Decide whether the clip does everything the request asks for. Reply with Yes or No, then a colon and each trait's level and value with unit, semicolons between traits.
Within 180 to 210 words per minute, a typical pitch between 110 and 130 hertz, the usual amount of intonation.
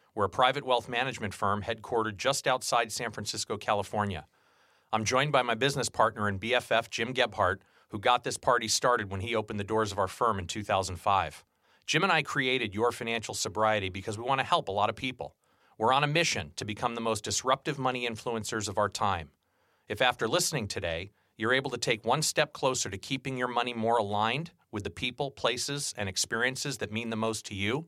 Yes: fast, 205 wpm; low, 115 Hz; average, 3.6 semitones